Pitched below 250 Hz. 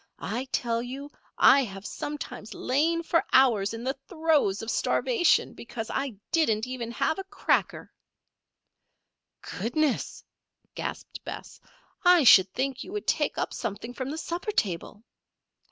No: very high, 260 Hz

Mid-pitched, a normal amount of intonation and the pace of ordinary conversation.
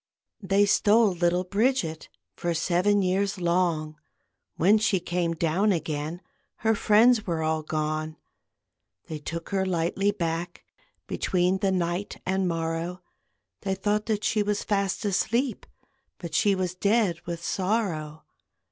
No: medium, 180 Hz; average, 3.5 semitones; slow, 130 wpm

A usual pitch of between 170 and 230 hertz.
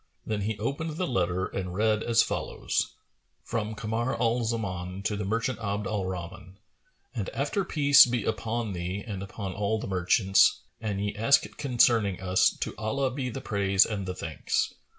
No: low, 105 Hz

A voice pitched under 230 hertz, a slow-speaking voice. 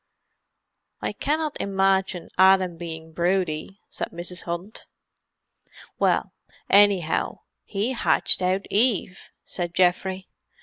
Yes: medium, 185 Hz; slow, 95 wpm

